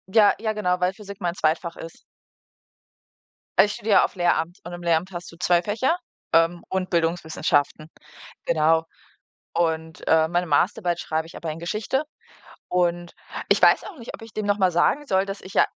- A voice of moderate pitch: Yes, medium, 175 Hz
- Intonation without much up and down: No, average, 3.3 semitones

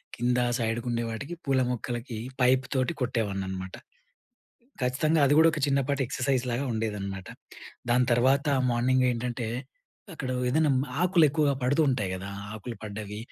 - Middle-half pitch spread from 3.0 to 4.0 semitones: Yes, average, 3.6 semitones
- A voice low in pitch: Yes, low, 125 Hz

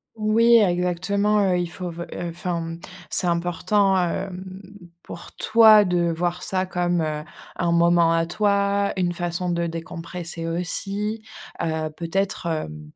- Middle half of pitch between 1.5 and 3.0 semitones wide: Yes, narrow, 2.6 semitones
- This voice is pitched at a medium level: Yes, medium, 175 Hz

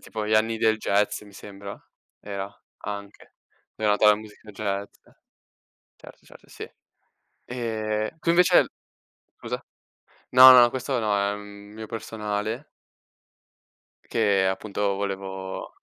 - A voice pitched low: Yes, low, 105 Hz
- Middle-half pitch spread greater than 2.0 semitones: No, narrow, 1.7 semitones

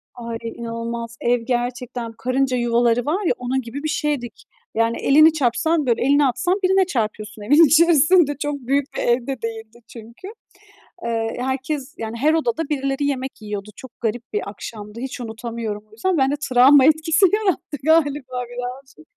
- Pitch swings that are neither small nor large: Yes, average, 4.0 semitones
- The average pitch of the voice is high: Yes, very high, 250 Hz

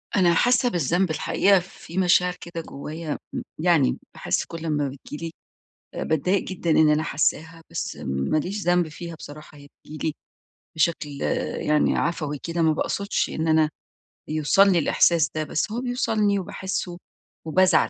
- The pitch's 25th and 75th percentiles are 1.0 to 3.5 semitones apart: Yes, average, 3.1 semitones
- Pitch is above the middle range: No, medium, 165 Hz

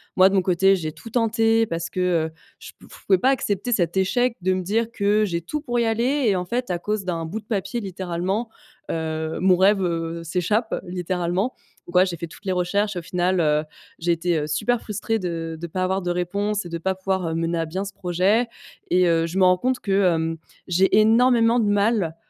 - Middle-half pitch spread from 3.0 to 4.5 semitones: Yes, average, 3.8 semitones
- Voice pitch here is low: No, medium, 185 Hz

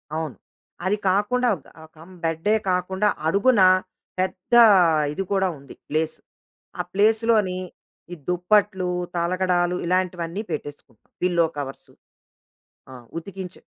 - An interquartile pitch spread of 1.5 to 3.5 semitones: Yes, average, 3.1 semitones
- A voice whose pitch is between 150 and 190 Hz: Yes, medium, 185 Hz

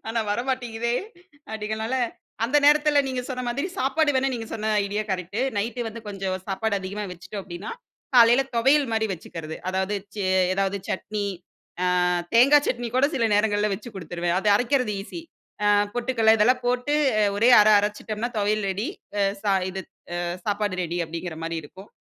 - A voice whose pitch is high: Yes, high, 215 Hz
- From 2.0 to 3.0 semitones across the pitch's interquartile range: No, average, 3.9 semitones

